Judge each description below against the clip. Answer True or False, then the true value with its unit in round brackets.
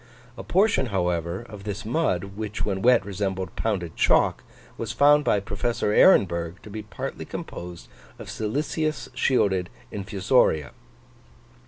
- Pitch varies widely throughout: False (4.3 semitones)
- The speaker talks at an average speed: False (130 wpm)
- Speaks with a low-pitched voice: True (100 Hz)